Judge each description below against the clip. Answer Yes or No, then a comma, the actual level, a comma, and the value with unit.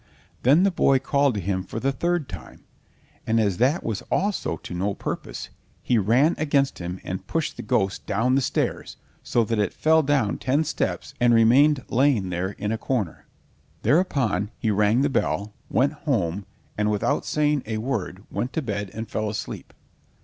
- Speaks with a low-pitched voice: Yes, low, 115 Hz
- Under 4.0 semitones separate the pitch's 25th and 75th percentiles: No, wide, 5.6 semitones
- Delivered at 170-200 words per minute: Yes, average, 180 wpm